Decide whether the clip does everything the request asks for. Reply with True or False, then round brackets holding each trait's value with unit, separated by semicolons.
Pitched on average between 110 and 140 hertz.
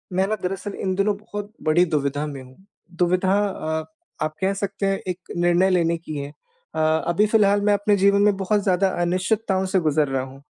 False (185 Hz)